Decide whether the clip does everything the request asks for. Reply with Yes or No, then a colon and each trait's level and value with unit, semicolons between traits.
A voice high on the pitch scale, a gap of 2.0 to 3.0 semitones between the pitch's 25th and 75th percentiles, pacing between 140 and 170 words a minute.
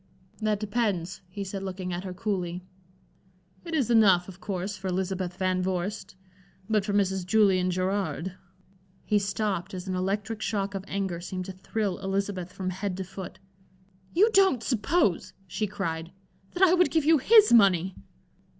Yes: high, 195 Hz; narrow, 2.4 semitones; average, 160 wpm